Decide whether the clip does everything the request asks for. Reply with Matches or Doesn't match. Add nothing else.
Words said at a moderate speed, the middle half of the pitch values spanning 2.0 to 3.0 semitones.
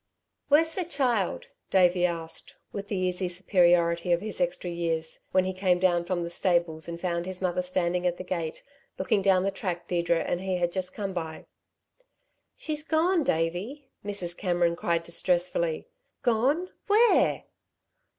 Matches